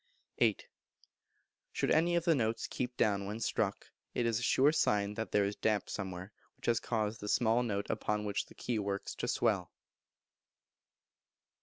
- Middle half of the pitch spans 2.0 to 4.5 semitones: Yes, average, 2.8 semitones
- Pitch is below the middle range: Yes, low, 110 Hz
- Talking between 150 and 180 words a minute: Yes, average, 170 wpm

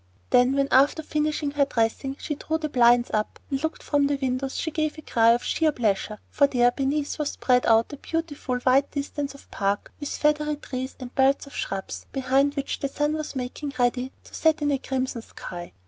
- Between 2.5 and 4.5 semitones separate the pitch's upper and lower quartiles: Yes, average, 3.0 semitones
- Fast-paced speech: Yes, fast, 210 wpm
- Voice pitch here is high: Yes, very high, 275 Hz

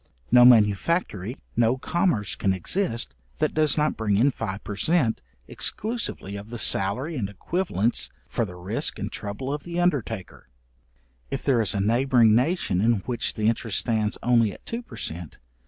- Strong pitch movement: Yes, wide, 5.7 semitones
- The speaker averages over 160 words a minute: Yes, average, 170 wpm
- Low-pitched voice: Yes, low, 115 Hz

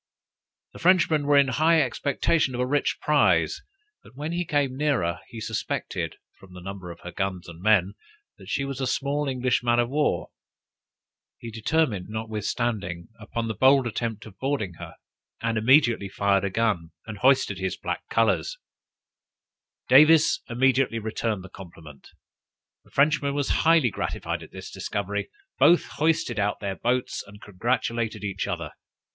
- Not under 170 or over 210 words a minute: No, average, 155 wpm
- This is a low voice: Yes, low, 115 Hz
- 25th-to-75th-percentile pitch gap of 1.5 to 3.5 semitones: No, wide, 5.6 semitones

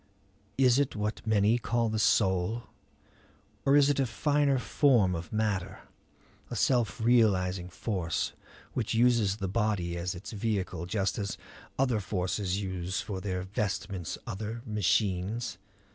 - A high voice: No, low, 105 Hz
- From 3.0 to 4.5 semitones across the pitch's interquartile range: Yes, average, 3.9 semitones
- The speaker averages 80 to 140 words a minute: Yes, slow, 135 wpm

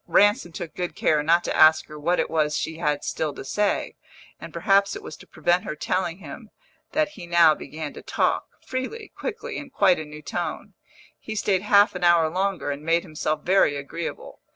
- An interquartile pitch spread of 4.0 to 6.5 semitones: Yes, average, 4.3 semitones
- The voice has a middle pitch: Yes, medium, 175 Hz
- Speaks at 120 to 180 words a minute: No, average, 200 wpm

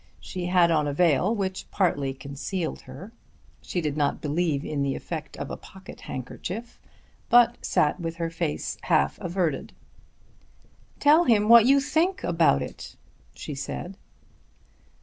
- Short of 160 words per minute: Yes, average, 145 wpm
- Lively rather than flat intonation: Yes, wide, 5.8 semitones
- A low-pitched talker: No, medium, 170 Hz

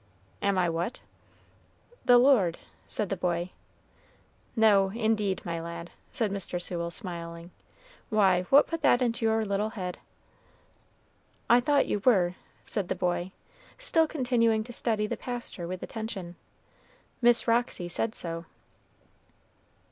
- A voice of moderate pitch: No, high, 205 Hz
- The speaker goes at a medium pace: No, slow, 130 wpm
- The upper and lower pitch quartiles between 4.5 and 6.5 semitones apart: Yes, average, 4.9 semitones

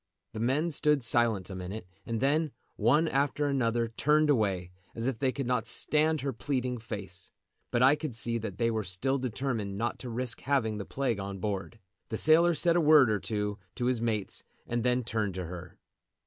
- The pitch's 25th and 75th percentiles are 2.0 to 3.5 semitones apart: No, average, 4.5 semitones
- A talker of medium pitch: No, low, 120 Hz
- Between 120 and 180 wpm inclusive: No, average, 200 wpm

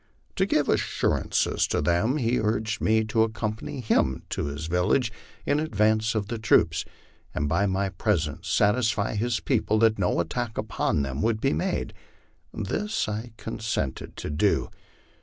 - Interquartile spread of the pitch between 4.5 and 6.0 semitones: No, average, 4.1 semitones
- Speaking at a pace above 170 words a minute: No, average, 155 wpm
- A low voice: Yes, low, 110 Hz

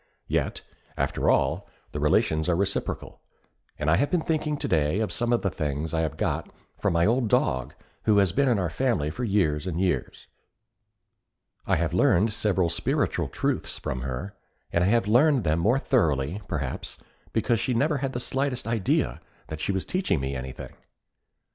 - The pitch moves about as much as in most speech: No, wide, 7.5 semitones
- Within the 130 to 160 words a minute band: No, average, 180 wpm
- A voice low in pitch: Yes, very low, 95 Hz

